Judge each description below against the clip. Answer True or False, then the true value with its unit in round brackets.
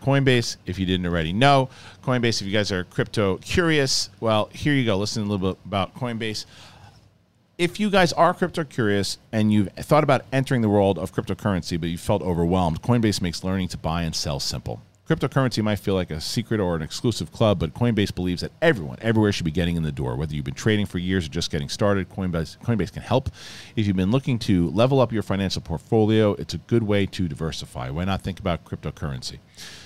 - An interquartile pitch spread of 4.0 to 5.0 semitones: True (4.6 semitones)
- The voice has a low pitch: True (100 Hz)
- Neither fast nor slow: False (215 wpm)